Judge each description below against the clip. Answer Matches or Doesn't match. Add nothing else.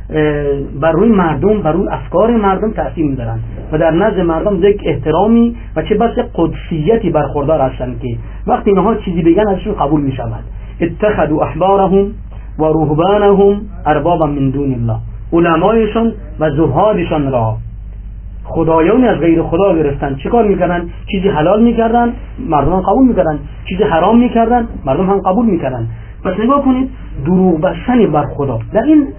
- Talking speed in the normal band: Matches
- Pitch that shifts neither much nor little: Doesn't match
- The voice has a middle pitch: Matches